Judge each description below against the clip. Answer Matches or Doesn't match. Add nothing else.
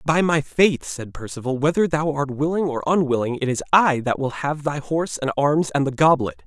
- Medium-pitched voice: Matches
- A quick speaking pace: Matches